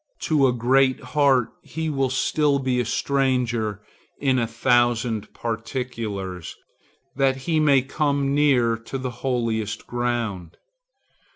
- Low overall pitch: Yes, low, 125 Hz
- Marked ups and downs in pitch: No, average, 2.9 semitones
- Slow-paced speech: Yes, slow, 120 wpm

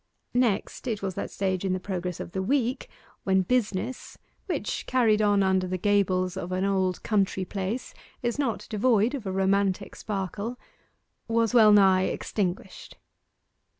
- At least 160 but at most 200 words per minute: No, average, 150 wpm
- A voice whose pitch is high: Yes, high, 200 Hz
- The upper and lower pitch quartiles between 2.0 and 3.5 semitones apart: Yes, average, 3.0 semitones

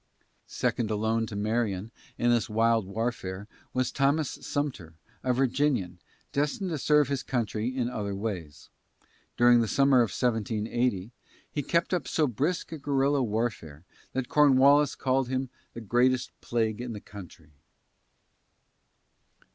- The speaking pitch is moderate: No, low, 120 Hz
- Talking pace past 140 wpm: No, slow, 135 wpm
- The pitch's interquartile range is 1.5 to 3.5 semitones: No, average, 4.1 semitones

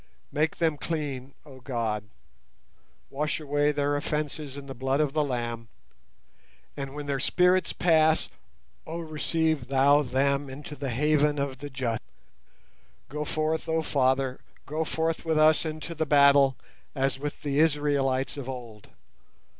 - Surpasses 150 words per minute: No, average, 145 wpm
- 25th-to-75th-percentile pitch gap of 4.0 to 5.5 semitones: No, narrow, 2.5 semitones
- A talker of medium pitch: Yes, medium, 145 Hz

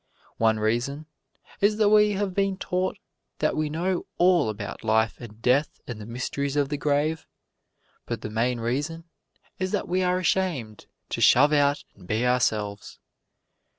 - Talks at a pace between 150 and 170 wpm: Yes, average, 160 wpm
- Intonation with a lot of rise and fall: Yes, wide, 7.9 semitones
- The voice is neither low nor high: Yes, medium, 145 Hz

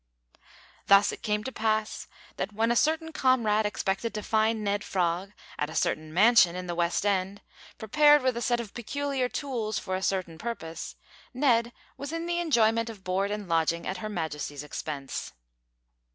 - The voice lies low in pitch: No, high, 210 Hz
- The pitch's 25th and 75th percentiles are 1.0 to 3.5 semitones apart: No, average, 4.5 semitones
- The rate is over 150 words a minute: Yes, average, 175 wpm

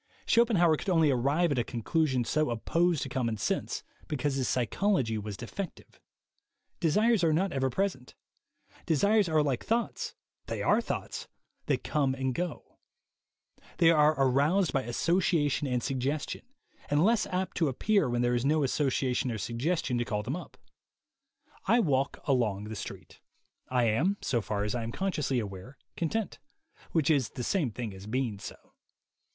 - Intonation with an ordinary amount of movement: No, wide, 5.7 semitones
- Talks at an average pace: Yes, average, 165 wpm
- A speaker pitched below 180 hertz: Yes, medium, 140 Hz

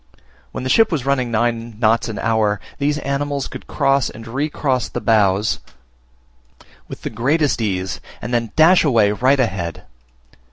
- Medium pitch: No, low, 120 Hz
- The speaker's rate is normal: Yes, average, 160 wpm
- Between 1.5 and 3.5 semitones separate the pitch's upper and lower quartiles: No, average, 4.2 semitones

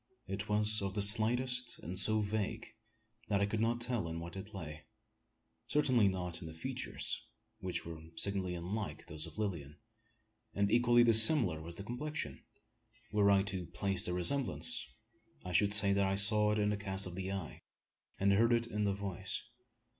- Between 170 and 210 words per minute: Yes, average, 180 wpm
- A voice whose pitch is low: Yes, low, 100 Hz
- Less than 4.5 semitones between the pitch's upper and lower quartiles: Yes, average, 3.1 semitones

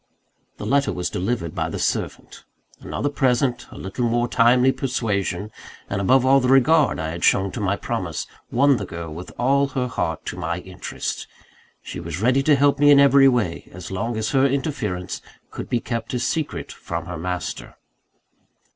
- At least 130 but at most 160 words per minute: No, average, 180 wpm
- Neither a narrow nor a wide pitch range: No, wide, 6.7 semitones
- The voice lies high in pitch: No, low, 120 Hz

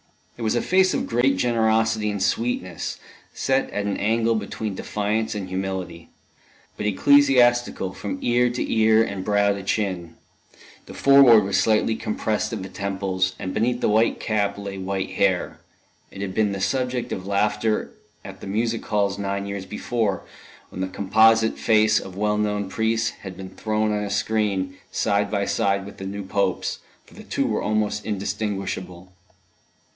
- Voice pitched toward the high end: No, low, 105 Hz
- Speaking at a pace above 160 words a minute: Yes, average, 170 wpm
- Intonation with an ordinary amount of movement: No, narrow, 2.3 semitones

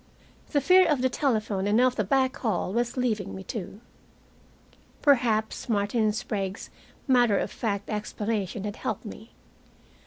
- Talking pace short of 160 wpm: Yes, average, 145 wpm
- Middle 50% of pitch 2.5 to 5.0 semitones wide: Yes, average, 3.6 semitones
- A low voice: No, high, 220 Hz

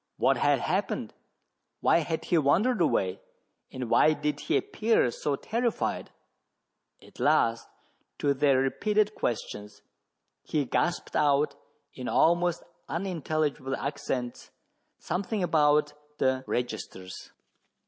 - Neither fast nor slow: No, slow, 110 wpm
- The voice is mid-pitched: Yes, medium, 150 Hz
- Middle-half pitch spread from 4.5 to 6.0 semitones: Yes, average, 4.9 semitones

